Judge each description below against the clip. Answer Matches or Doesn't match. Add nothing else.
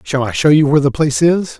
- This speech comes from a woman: Doesn't match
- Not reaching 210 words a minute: Doesn't match